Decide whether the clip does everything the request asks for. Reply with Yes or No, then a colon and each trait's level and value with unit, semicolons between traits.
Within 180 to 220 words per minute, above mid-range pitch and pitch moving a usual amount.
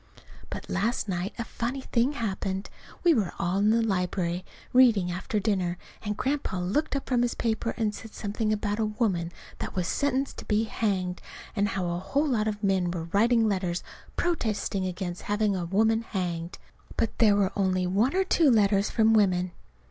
Yes: average, 185 wpm; high, 205 Hz; average, 3.6 semitones